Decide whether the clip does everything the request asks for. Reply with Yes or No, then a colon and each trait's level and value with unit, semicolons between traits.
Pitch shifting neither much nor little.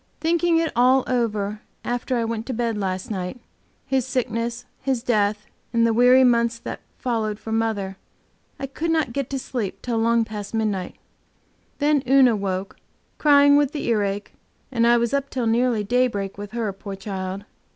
Yes: average, 3.6 semitones